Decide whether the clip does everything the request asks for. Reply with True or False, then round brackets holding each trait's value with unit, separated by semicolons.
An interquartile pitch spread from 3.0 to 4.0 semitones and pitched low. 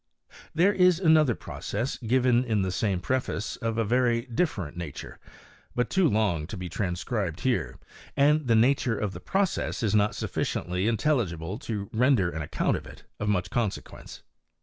False (5.0 semitones; 115 Hz)